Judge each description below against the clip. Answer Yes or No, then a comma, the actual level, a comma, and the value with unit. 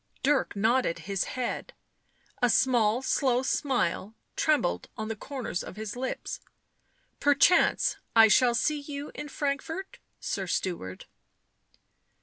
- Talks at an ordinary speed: No, slow, 125 wpm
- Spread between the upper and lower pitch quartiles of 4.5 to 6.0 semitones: Yes, average, 5.0 semitones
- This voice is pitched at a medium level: No, very high, 250 Hz